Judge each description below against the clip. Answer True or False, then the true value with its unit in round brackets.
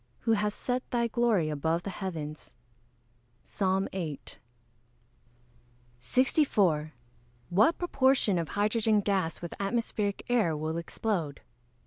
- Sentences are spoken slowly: True (105 wpm)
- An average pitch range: False (5.8 semitones)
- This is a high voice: True (200 Hz)